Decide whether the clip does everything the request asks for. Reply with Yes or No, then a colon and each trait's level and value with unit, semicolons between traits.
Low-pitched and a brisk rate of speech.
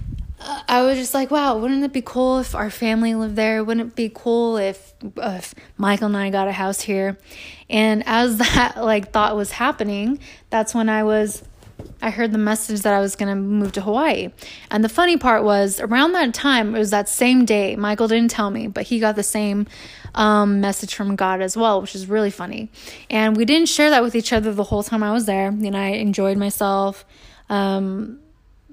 No: high, 215 Hz; fast, 210 wpm